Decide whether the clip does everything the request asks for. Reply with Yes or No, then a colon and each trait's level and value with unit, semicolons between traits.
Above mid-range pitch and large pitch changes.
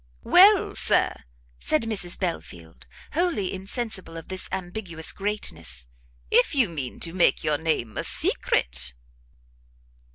No: medium, 175 Hz; wide, 6.7 semitones